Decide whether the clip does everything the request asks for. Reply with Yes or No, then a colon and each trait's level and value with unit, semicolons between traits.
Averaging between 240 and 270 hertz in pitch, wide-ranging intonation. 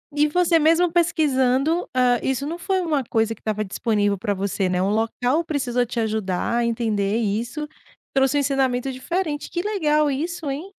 Yes: very high, 265 Hz; wide, 5.9 semitones